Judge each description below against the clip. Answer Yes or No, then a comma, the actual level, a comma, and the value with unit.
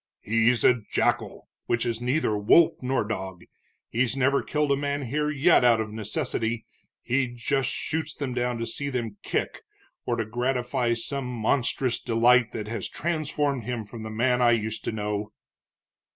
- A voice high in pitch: No, low, 120 Hz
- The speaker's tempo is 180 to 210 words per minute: No, average, 165 wpm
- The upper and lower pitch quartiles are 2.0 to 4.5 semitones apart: Yes, average, 3.3 semitones